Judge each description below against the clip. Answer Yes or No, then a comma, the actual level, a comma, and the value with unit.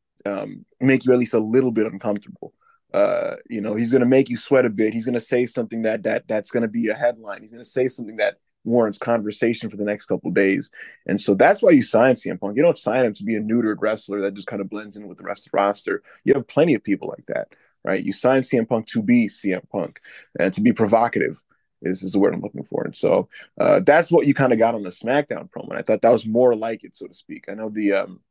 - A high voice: No, low, 115 Hz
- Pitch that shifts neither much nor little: Yes, average, 3.1 semitones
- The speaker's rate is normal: No, fast, 270 wpm